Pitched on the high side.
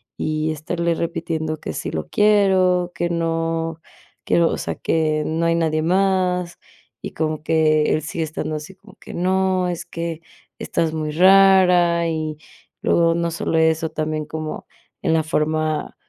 No: medium, 165 Hz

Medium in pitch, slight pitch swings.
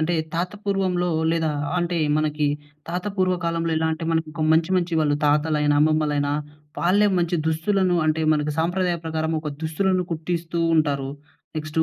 Yes: medium, 160 Hz; narrow, 2.2 semitones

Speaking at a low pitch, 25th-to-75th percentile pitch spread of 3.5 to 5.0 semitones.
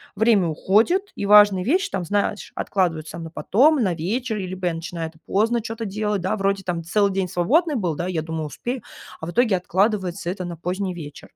No: high, 190 Hz; average, 4.0 semitones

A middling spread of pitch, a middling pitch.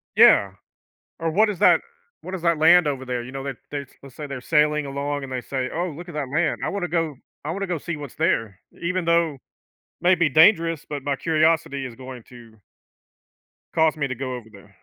Yes: average, 4.1 semitones; medium, 150 Hz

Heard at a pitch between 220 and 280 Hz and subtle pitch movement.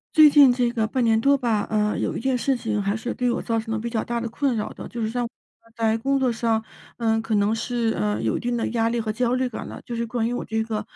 Yes: high, 230 Hz; narrow, 1.7 semitones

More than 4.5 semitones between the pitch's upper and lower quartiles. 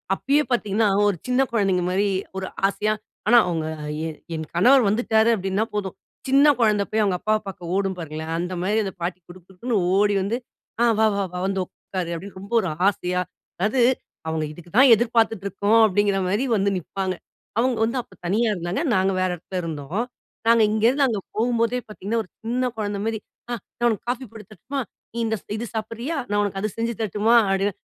No: average, 3.5 semitones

